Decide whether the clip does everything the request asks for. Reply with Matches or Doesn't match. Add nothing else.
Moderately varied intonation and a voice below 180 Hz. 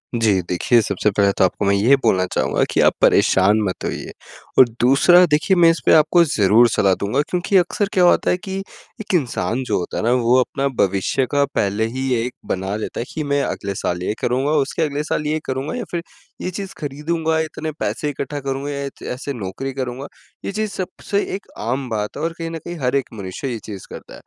Doesn't match